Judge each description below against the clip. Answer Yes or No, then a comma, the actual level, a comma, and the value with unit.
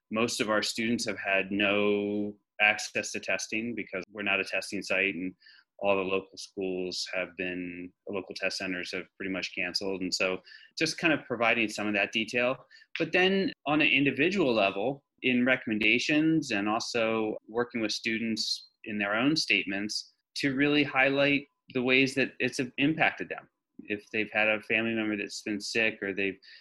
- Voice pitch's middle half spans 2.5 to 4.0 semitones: No, average, 4.4 semitones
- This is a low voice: Yes, low, 110 Hz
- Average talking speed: Yes, average, 175 wpm